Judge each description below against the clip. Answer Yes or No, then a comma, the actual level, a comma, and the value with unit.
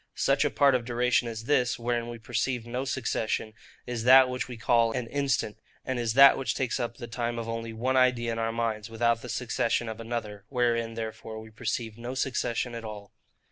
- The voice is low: Yes, low, 120 Hz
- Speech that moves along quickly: Yes, fast, 210 wpm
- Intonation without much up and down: Yes, narrow, 1.6 semitones